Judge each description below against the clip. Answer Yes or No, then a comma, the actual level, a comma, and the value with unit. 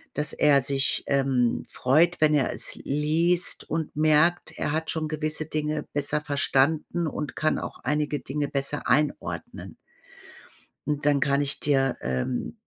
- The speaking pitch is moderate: Yes, medium, 150 Hz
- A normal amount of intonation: No, narrow, 1.9 semitones